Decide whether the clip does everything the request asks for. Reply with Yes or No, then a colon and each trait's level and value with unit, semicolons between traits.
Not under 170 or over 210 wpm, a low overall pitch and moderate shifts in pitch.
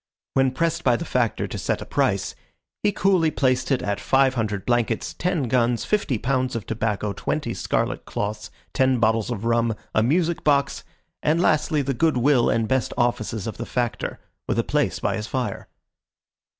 Yes: average, 180 wpm; low, 125 Hz; average, 3.9 semitones